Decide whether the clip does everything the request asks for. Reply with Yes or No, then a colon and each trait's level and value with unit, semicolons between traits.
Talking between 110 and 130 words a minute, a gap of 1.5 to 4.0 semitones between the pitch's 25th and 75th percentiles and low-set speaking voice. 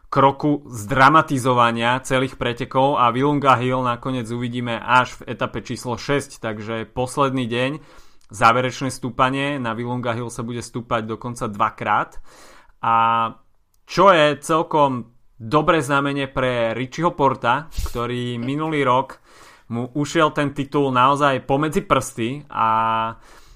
Yes: average, 120 wpm; average, 2.9 semitones; low, 125 Hz